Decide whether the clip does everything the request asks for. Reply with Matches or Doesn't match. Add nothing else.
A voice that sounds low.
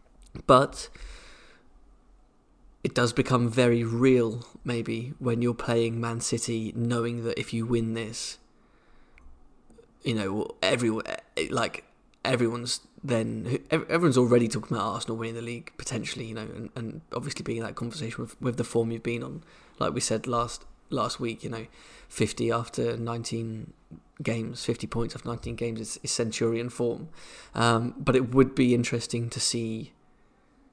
Matches